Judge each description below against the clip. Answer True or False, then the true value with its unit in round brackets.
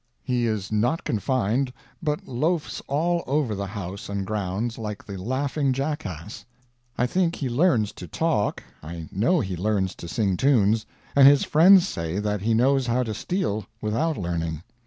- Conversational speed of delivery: True (165 wpm)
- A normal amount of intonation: False (6.0 semitones)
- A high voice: False (115 Hz)